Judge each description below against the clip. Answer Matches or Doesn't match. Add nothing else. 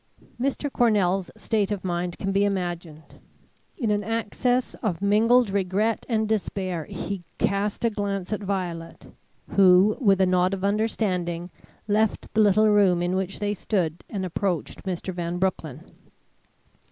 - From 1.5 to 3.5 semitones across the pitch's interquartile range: Matches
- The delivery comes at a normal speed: Matches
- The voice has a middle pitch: Doesn't match